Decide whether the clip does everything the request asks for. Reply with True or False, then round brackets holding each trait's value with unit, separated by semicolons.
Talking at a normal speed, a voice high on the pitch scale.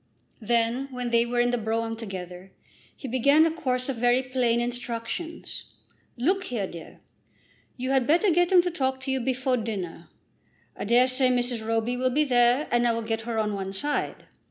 True (190 wpm; 245 Hz)